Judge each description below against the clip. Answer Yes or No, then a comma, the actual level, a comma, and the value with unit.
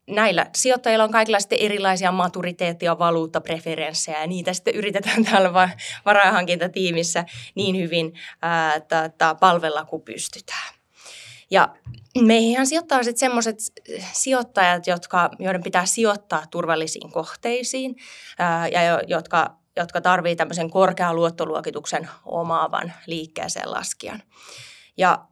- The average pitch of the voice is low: No, medium, 180 Hz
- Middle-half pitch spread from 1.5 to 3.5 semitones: No, average, 3.9 semitones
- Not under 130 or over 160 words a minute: No, average, 100 wpm